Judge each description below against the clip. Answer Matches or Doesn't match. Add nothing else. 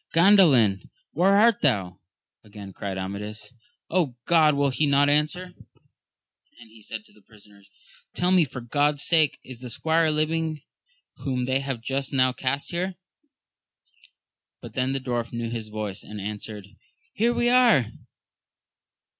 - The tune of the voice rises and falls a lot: Matches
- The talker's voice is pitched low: Matches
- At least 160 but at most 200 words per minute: Doesn't match